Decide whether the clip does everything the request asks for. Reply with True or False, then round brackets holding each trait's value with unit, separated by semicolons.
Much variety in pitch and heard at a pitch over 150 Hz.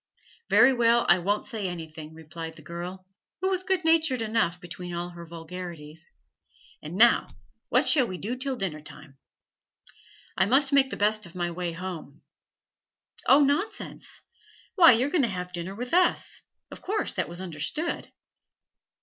True (7.4 semitones; 185 Hz)